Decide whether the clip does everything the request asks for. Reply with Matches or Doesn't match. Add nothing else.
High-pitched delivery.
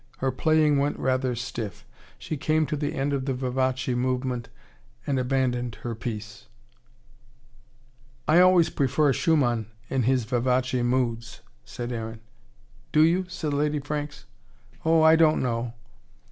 Doesn't match